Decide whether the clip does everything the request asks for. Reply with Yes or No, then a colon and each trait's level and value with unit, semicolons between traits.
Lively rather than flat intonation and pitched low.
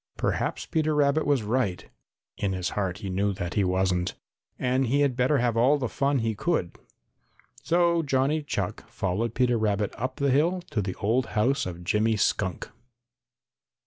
Yes: wide, 6.0 semitones; low, 115 Hz